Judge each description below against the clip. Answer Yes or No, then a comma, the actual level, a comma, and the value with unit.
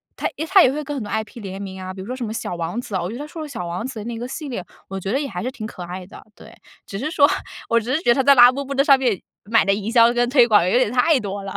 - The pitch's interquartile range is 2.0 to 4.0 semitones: No, average, 5.1 semitones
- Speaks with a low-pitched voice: No, high, 235 Hz